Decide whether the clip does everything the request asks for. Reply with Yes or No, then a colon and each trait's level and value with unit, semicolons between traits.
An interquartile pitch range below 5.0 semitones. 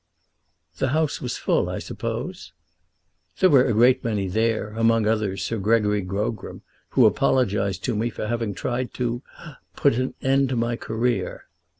Yes: average, 2.8 semitones